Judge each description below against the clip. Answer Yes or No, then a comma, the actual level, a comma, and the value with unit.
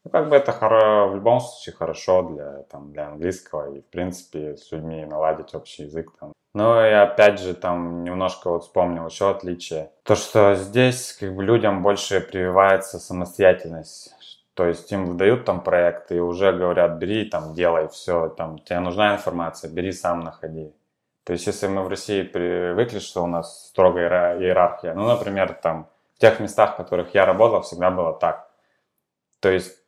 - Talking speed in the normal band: No, fast, 170 wpm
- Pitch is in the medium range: No, very low, 90 Hz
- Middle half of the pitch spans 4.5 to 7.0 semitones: No, average, 2.8 semitones